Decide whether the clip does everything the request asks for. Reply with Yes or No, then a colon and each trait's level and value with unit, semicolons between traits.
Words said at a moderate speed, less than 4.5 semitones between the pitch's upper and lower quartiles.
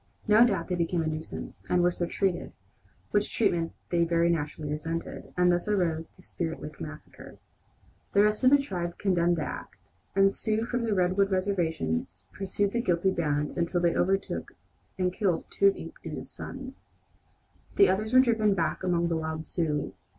Yes: average, 175 wpm; average, 3.4 semitones